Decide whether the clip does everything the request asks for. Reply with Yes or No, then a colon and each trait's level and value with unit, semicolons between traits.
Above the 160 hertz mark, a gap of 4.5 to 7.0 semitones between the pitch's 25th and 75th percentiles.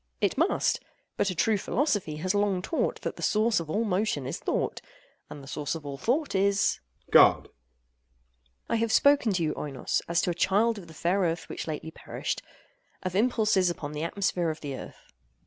Yes: medium, 185 Hz; average, 5.1 semitones